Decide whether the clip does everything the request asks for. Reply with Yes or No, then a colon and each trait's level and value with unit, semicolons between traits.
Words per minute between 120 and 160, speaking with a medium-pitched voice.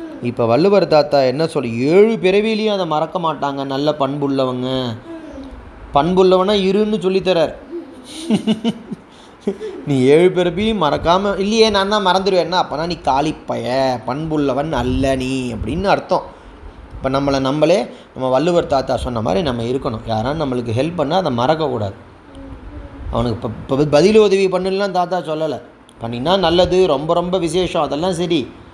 Yes: fast, 130 wpm; medium, 155 Hz